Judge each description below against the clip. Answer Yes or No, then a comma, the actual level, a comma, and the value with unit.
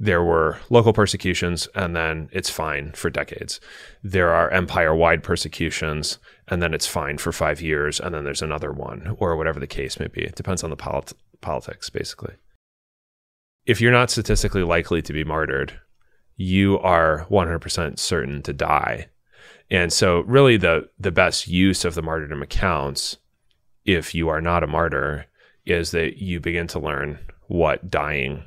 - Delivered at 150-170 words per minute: Yes, average, 165 wpm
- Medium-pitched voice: No, very low, 85 Hz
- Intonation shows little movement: No, average, 3.4 semitones